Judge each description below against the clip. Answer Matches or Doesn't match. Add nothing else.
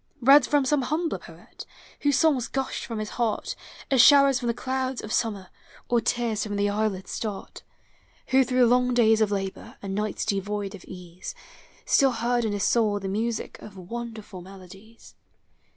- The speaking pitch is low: Doesn't match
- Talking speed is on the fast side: Doesn't match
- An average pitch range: Matches